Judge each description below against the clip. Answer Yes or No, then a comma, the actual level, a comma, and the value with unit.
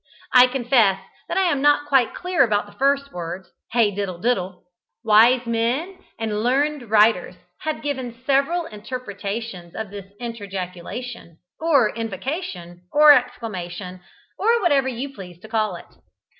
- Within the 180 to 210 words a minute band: No, average, 140 wpm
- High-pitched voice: Yes, high, 230 Hz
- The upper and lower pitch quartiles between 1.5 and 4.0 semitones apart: No, wide, 5.6 semitones